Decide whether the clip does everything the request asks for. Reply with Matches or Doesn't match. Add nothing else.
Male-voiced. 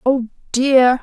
Doesn't match